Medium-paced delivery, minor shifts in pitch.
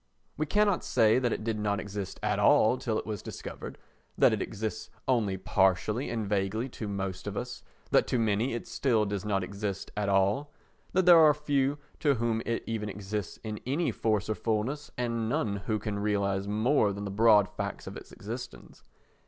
No: average, 195 wpm; average, 3.2 semitones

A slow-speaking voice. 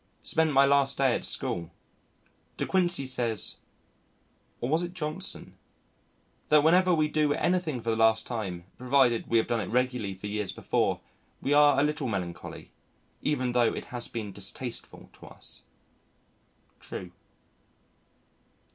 No: average, 145 wpm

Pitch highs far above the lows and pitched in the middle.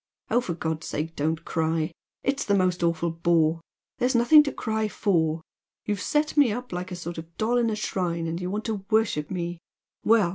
No: average, 5.0 semitones; medium, 180 Hz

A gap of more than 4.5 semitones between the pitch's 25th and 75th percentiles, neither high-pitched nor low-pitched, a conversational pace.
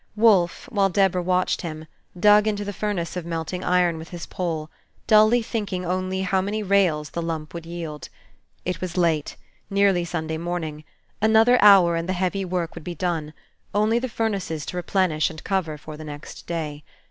No: average, 3.5 semitones; medium, 180 Hz; average, 180 wpm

